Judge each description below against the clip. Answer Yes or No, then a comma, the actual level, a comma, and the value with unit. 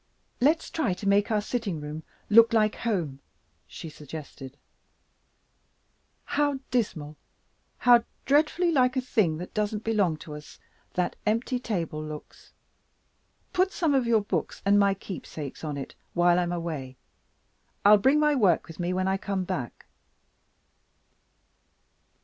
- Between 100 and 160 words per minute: Yes, average, 140 wpm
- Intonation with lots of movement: Yes, wide, 6.7 semitones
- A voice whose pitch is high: Yes, high, 200 Hz